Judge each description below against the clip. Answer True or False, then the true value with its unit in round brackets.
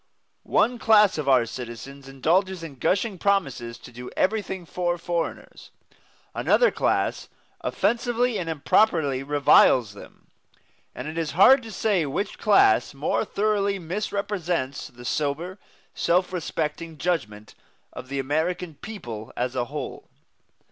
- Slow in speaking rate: True (125 wpm)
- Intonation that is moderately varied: False (6.6 semitones)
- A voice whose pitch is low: False (165 Hz)